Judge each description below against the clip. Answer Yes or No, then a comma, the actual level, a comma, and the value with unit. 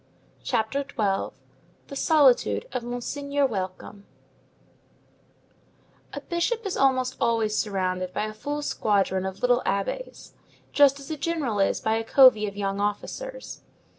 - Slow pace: Yes, slow, 130 wpm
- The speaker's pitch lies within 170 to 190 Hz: No, high, 235 Hz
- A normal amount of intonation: No, wide, 5.9 semitones